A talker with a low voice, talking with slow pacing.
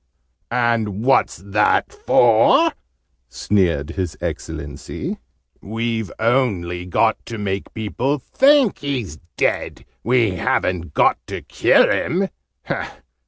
Yes: low, 110 Hz; slow, 100 wpm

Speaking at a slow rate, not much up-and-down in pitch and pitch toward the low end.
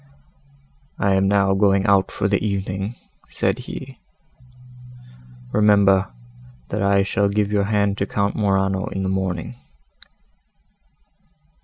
Yes: slow, 120 wpm; narrow, 0.9 semitones; low, 100 Hz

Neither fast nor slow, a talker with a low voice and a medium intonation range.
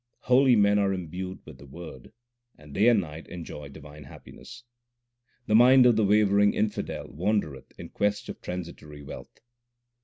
No: average, 155 wpm; very low, 95 Hz; wide, 5.9 semitones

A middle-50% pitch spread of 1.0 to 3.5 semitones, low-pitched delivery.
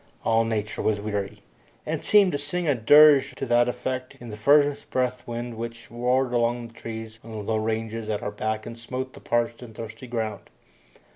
Yes: narrow, 2.5 semitones; low, 115 Hz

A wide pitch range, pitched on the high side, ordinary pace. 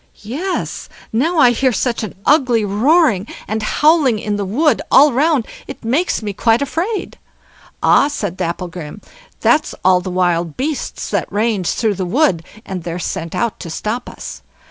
Yes: wide, 7.3 semitones; high, 225 Hz; average, 165 wpm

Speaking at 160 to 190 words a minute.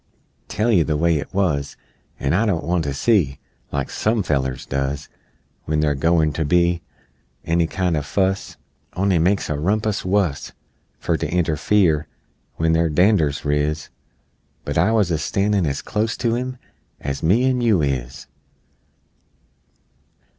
No: average, 150 wpm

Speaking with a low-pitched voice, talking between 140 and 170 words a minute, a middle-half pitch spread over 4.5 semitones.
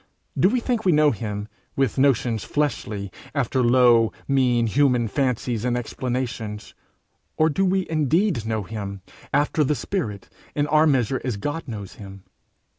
Yes: low, 125 Hz; average, 150 wpm; average, 5.0 semitones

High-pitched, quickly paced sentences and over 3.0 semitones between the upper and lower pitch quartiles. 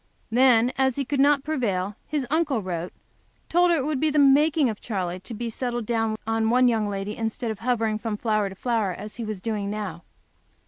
Yes: high, 225 Hz; fast, 215 wpm; average, 4.1 semitones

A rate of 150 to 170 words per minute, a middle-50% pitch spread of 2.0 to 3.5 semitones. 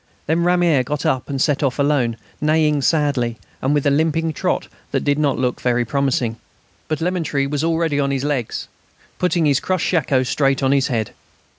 No: average, 185 wpm; average, 3.1 semitones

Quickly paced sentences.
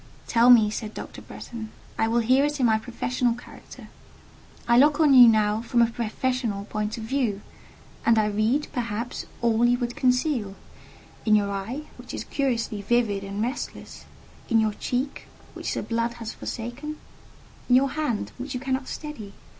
No: average, 170 wpm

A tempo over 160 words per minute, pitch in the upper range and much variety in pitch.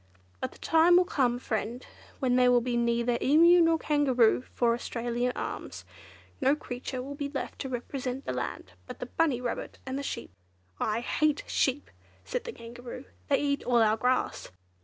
No: average, 180 wpm; very high, 250 Hz; average, 3.1 semitones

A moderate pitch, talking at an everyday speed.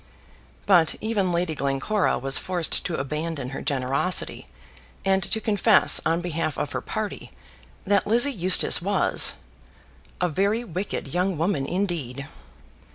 No: medium, 175 Hz; slow, 130 wpm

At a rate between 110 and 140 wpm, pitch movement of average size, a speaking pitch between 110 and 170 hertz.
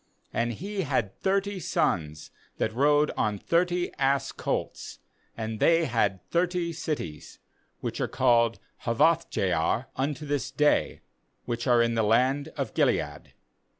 No: slow, 135 wpm; wide, 6.5 semitones; low, 135 Hz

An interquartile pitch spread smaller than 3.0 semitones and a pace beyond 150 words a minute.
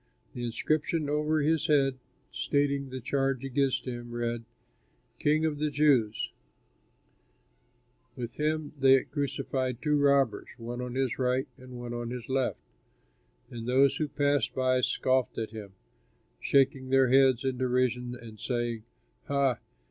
No: narrow, 2.5 semitones; average, 140 wpm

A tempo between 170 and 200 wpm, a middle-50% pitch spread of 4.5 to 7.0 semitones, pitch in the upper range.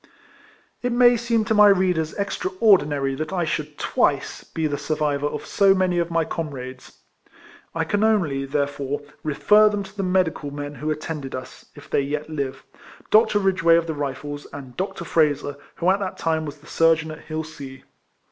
No: average, 185 wpm; average, 4.9 semitones; medium, 160 Hz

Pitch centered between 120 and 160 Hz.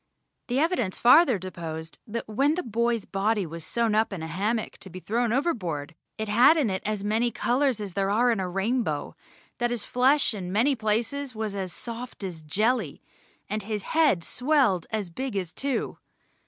No: high, 220 Hz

